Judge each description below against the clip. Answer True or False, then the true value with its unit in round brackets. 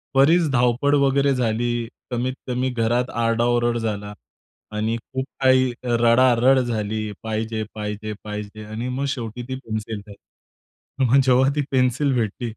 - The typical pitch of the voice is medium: False (120 Hz)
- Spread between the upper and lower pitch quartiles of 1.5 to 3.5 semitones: True (2.9 semitones)